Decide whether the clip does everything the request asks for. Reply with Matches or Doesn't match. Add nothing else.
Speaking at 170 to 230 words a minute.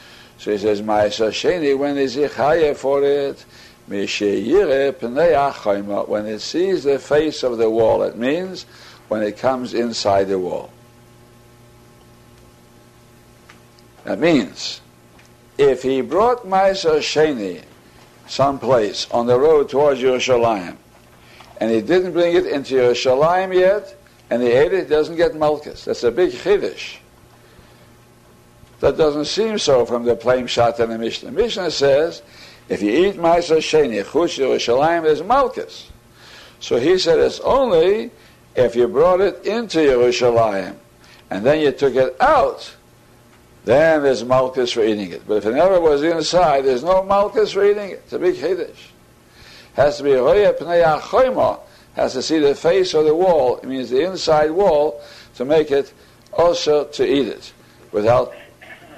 Doesn't match